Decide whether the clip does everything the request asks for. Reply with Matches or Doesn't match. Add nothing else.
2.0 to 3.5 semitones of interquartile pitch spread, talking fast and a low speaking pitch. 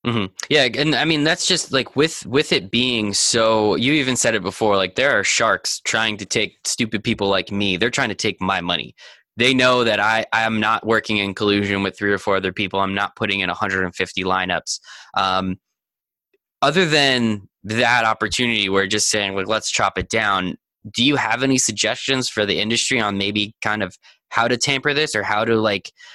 Doesn't match